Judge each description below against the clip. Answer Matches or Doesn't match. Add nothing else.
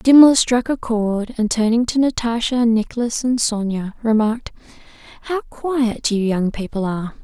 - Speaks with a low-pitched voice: Doesn't match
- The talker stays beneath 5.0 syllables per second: Matches